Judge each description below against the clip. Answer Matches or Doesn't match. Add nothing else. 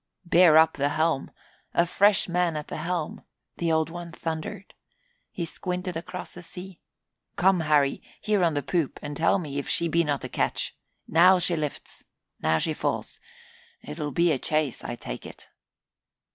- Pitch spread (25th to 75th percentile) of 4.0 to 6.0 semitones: Doesn't match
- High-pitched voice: Doesn't match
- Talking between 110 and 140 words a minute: Doesn't match